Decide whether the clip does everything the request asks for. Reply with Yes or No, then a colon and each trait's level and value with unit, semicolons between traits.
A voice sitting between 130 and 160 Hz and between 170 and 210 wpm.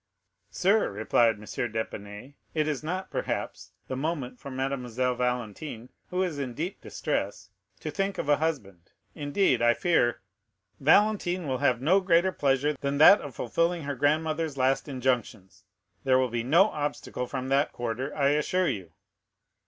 No: medium, 140 Hz; average, 160 wpm